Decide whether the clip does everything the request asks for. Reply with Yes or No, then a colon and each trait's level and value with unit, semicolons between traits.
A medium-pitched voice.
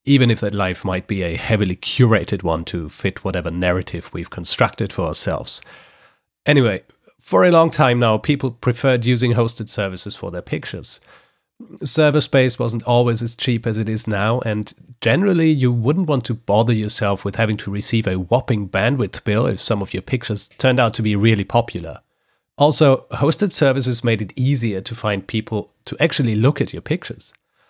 No: low, 115 Hz